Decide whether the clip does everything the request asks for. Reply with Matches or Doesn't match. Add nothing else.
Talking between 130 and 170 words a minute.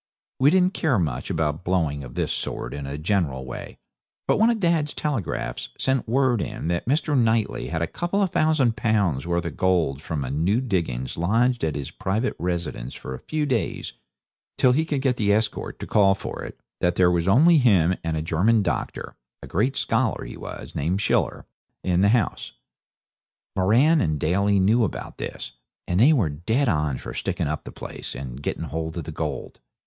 Doesn't match